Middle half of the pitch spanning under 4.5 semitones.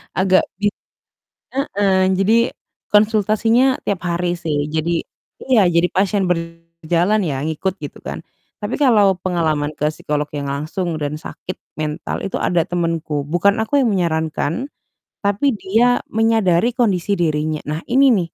No: average, 4.8 semitones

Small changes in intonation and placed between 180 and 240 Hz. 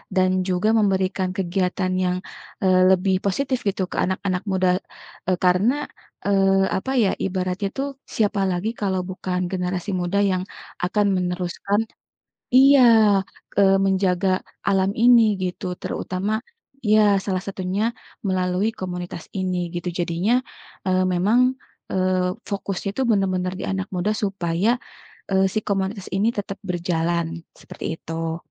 Yes: narrow, 1.6 semitones; medium, 185 Hz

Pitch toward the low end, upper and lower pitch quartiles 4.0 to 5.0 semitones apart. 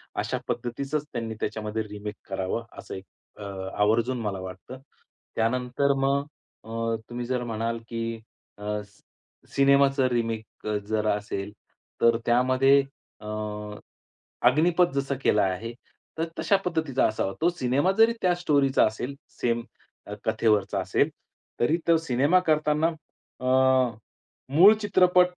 Yes: low, 125 Hz; average, 4.5 semitones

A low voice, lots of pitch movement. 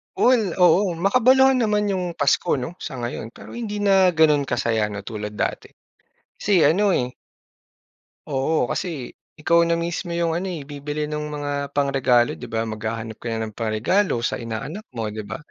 No: medium, 150 Hz; wide, 7.4 semitones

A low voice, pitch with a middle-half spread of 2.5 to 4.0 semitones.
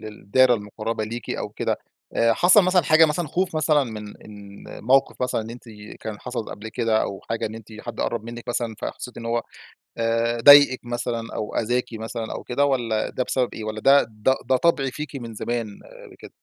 Yes: low, 120 Hz; average, 3.0 semitones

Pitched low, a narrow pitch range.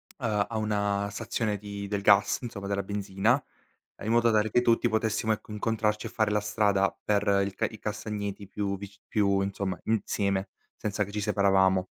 Yes: low, 105 Hz; narrow, 1.5 semitones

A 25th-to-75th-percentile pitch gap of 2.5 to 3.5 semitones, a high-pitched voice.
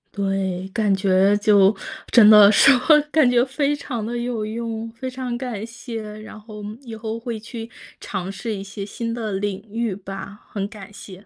Yes: average, 3.0 semitones; high, 215 Hz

